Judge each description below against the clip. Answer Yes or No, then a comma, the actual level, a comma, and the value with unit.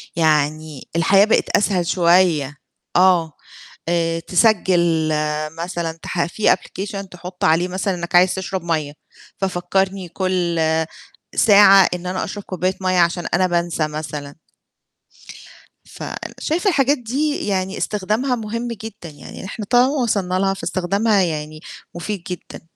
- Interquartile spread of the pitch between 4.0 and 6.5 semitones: No, average, 2.9 semitones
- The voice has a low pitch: No, medium, 185 Hz